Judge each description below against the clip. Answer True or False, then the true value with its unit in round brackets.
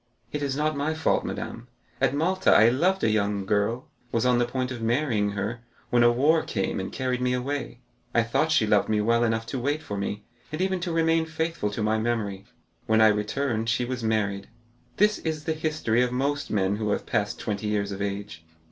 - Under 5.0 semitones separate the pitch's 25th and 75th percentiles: False (5.5 semitones)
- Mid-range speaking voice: False (120 Hz)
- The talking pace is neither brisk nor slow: False (210 wpm)